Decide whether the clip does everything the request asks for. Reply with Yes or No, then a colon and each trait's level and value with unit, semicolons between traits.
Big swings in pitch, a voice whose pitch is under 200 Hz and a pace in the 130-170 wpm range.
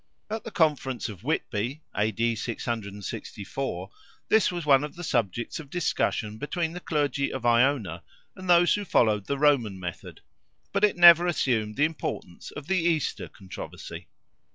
Yes: wide, 7.6 semitones; low, 135 Hz; average, 150 wpm